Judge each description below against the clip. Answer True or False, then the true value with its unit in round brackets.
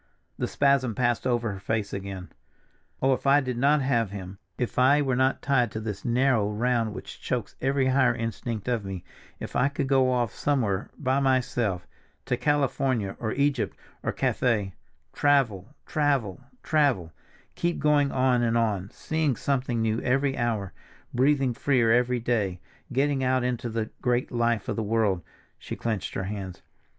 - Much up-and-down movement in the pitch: False (3.7 semitones)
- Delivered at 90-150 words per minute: False (160 wpm)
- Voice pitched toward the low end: True (120 Hz)